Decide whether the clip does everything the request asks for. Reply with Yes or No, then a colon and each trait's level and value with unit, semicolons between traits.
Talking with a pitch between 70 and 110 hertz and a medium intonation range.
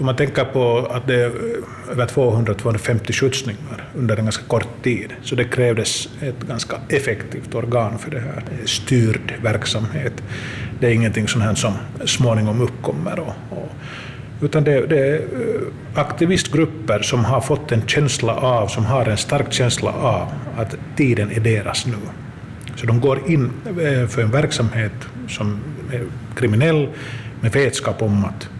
No: low, 120 Hz; average, 3.0 semitones